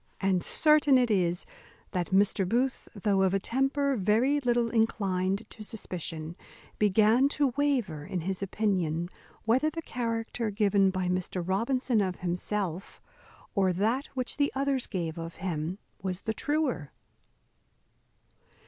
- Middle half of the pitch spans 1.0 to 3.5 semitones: No, average, 5.3 semitones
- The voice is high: Yes, high, 205 Hz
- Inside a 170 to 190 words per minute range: No, slow, 135 wpm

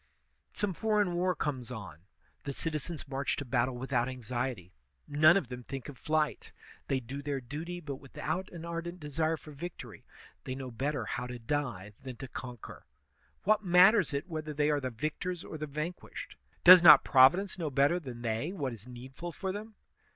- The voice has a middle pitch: Yes, medium, 145 Hz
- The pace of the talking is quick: No, average, 180 wpm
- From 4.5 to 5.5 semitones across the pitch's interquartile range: Yes, average, 5.0 semitones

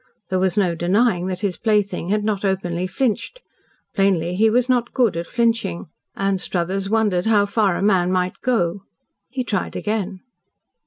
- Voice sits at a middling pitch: No, high, 195 Hz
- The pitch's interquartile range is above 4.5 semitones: No, average, 3.3 semitones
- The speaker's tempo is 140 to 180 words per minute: Yes, average, 160 wpm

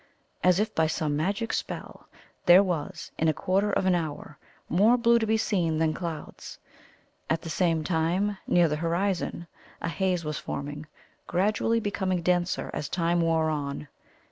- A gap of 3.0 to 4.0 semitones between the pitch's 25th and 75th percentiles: Yes, average, 3.4 semitones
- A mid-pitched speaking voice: Yes, medium, 175 Hz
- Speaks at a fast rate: No, average, 165 wpm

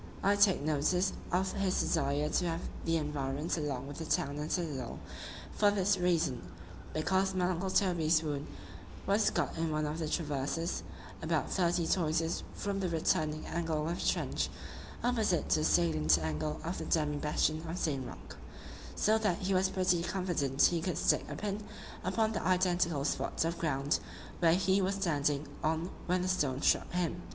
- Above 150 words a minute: Yes, average, 170 wpm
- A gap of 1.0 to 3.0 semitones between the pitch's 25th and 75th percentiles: No, average, 3.8 semitones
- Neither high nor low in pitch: Yes, medium, 165 Hz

